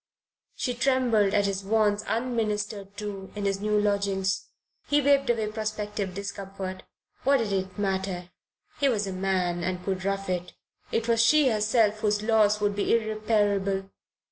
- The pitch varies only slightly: Yes, narrow, 2.2 semitones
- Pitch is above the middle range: Yes, high, 205 Hz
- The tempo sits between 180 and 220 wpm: No, average, 155 wpm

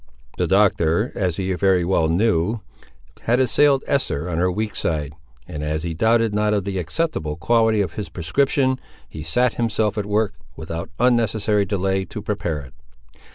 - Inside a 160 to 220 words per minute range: Yes, average, 165 wpm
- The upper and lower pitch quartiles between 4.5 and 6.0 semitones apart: Yes, average, 5.1 semitones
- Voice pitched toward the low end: Yes, low, 100 Hz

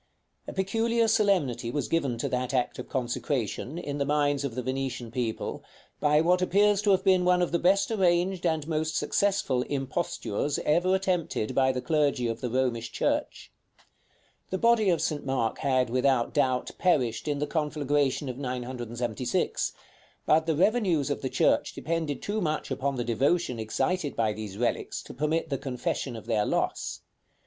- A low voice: No, medium, 145 Hz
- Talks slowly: No, average, 170 wpm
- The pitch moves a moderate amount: No, wide, 5.7 semitones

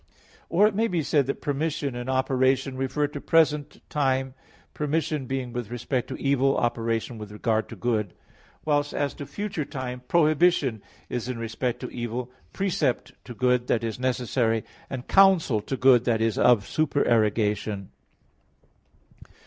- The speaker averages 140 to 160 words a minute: Yes, average, 150 wpm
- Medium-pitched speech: No, low, 130 Hz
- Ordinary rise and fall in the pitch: Yes, average, 3.7 semitones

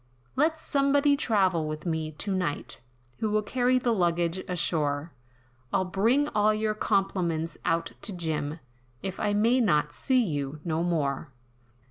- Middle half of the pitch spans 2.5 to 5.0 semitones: No, wide, 5.4 semitones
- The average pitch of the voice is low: No, medium, 185 Hz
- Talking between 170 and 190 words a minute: No, average, 145 wpm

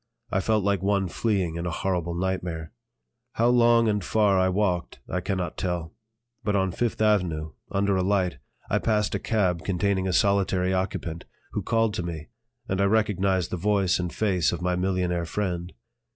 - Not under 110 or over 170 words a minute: No, average, 180 wpm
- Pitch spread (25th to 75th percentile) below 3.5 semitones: Yes, narrow, 2.5 semitones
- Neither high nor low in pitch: No, very low, 95 Hz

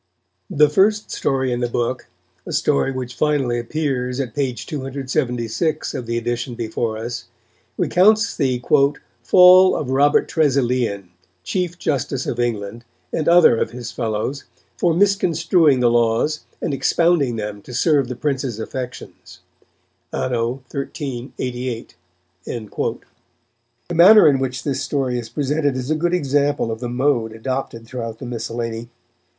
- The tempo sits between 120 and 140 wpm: Yes, slow, 135 wpm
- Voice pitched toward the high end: No, low, 130 Hz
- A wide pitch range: No, average, 3.8 semitones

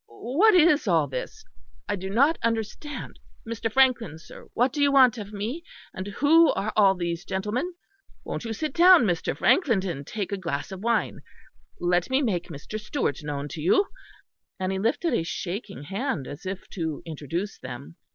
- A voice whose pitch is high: Yes, high, 205 Hz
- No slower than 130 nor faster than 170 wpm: No, average, 180 wpm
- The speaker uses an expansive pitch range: Yes, wide, 7.0 semitones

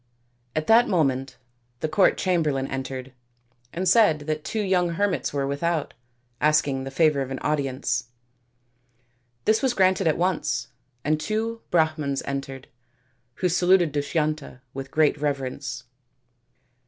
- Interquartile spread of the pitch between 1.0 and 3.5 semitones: No, average, 4.7 semitones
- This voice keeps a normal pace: No, slow, 130 wpm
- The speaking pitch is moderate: Yes, medium, 155 Hz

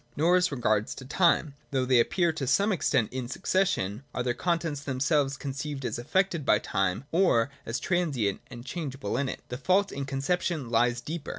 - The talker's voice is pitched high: No, medium, 140 Hz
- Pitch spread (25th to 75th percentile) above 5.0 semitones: Yes, wide, 5.5 semitones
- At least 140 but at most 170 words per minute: No, average, 180 wpm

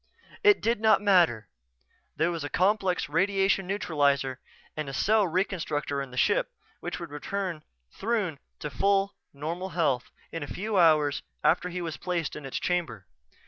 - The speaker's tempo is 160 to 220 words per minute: No, average, 150 wpm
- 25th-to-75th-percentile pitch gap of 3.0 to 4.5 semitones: No, average, 5.0 semitones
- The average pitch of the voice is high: No, medium, 170 Hz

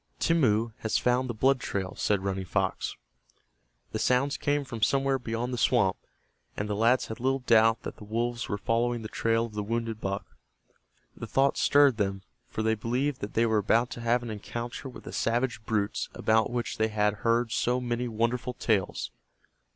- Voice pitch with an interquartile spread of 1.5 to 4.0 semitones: Yes, narrow, 2.4 semitones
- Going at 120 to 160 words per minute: No, average, 190 wpm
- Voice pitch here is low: Yes, low, 115 Hz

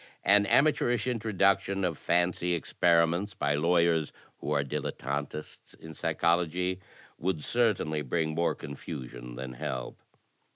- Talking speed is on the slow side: Yes, slow, 115 wpm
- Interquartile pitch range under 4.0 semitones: No, average, 4.6 semitones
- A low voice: Yes, very low, 85 Hz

